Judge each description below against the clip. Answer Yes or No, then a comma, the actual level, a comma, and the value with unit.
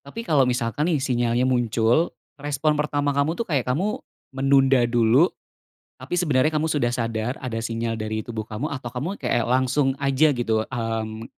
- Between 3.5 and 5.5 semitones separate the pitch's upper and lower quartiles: Yes, average, 3.8 semitones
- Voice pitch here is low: Yes, low, 130 Hz